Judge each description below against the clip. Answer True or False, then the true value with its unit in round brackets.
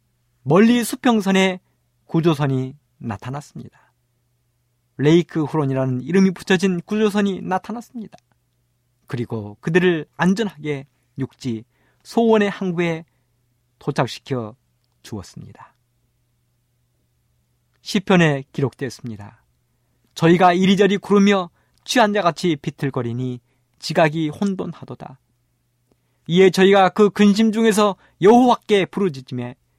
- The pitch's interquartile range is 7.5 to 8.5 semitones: True (7.8 semitones)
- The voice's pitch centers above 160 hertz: False (145 Hz)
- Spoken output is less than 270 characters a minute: True (250 characters per minute)